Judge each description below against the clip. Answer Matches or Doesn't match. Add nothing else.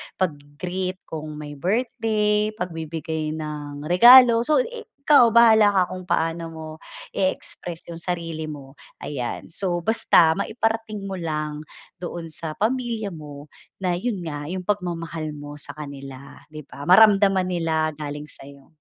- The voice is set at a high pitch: Doesn't match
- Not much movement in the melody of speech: Doesn't match